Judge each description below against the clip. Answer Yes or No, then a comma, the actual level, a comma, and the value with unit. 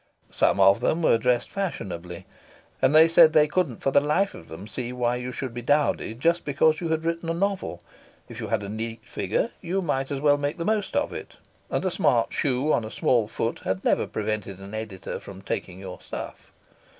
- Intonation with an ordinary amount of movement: No, wide, 6.9 semitones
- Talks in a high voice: No, low, 130 Hz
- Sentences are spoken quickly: Yes, fast, 215 wpm